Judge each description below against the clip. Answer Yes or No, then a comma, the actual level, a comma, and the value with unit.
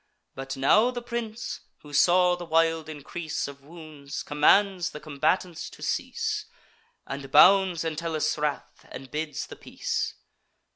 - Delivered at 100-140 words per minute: Yes, slow, 135 wpm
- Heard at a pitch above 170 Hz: No, medium, 160 Hz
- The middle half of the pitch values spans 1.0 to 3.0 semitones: No, average, 3.5 semitones